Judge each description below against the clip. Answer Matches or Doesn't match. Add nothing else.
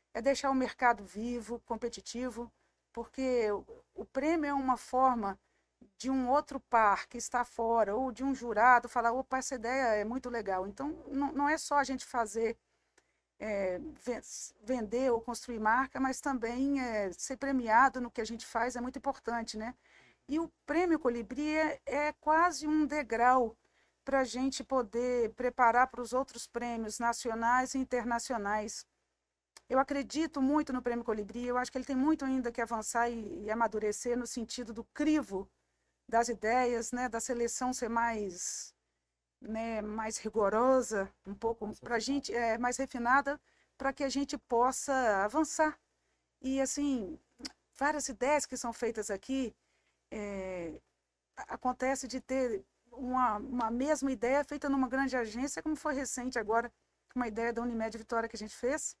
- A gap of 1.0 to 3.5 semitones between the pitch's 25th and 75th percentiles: Matches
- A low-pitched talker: Doesn't match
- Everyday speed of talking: Matches